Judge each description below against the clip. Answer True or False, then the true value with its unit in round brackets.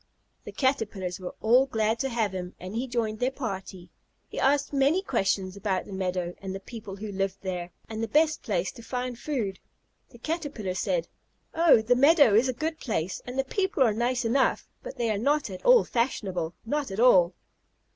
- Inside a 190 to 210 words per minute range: True (195 wpm)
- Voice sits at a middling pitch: False (225 Hz)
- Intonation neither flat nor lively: False (5.7 semitones)